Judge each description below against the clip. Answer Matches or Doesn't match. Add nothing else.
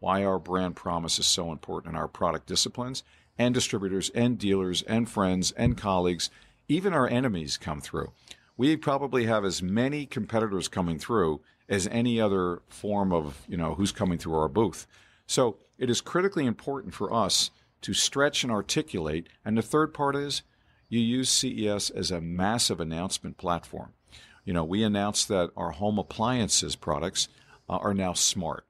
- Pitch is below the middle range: Matches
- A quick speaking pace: Doesn't match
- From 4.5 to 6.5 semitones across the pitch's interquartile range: Matches